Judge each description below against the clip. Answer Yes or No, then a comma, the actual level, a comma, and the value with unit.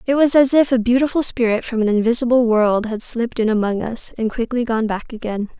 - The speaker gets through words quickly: Yes, fast, 225 wpm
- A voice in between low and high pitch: No, high, 235 Hz